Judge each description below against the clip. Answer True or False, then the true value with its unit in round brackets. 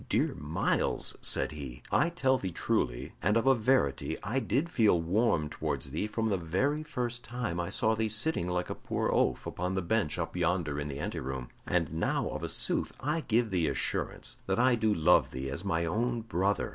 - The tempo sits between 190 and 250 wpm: True (205 wpm)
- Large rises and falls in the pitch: True (6.6 semitones)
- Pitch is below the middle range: True (100 Hz)